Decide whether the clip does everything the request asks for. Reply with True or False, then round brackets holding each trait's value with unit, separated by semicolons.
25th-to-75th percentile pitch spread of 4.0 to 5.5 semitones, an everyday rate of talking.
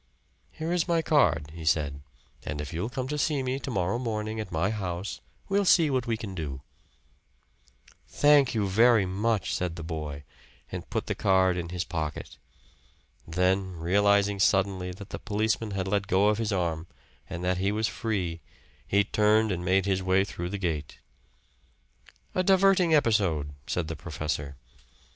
True (4.4 semitones; 170 wpm)